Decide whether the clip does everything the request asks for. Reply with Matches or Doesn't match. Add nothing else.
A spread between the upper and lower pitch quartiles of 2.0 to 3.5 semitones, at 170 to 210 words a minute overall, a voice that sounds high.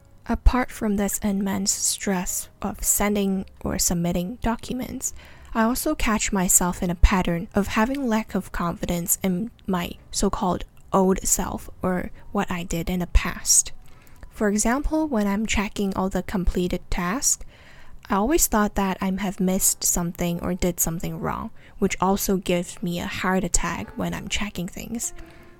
Doesn't match